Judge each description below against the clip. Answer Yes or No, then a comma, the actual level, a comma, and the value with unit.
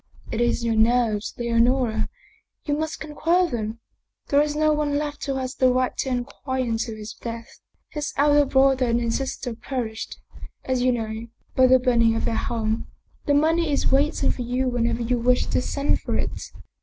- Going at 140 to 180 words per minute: No, average, 195 wpm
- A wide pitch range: No, average, 3.5 semitones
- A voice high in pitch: Yes, very high, 250 Hz